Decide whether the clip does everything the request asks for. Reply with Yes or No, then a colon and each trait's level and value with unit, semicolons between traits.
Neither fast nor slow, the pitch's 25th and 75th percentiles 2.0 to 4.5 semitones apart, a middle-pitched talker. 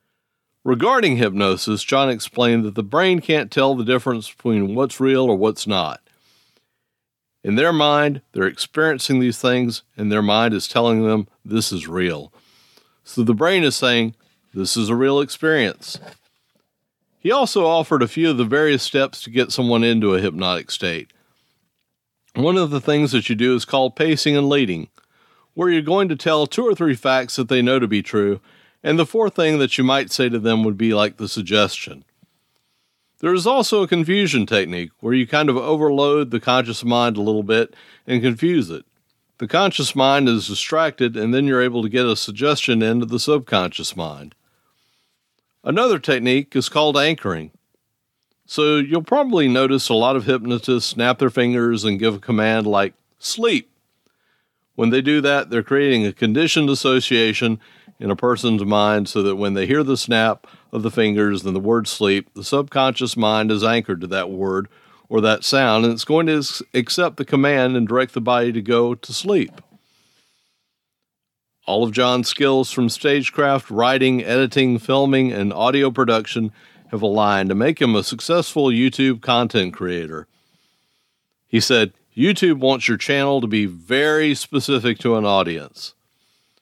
No: average, 170 wpm; average, 4.1 semitones; low, 125 Hz